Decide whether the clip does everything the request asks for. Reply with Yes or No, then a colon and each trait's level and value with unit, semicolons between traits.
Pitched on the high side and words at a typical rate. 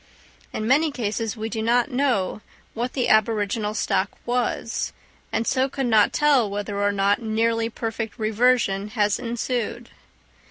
Yes: high, 225 Hz; average, 145 wpm